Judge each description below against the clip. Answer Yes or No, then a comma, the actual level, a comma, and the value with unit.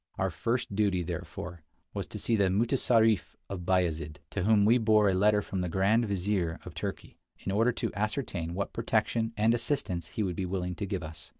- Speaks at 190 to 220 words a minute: Yes, average, 200 wpm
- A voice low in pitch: Yes, low, 100 Hz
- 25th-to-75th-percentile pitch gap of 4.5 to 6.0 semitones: No, average, 3.7 semitones